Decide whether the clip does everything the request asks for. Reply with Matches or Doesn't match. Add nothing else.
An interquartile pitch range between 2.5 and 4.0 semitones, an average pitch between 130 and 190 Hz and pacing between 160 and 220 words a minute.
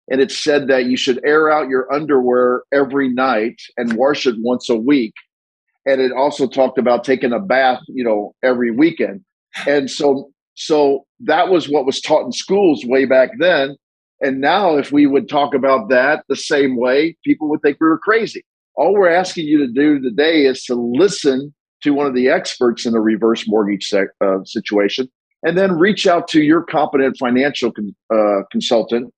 Matches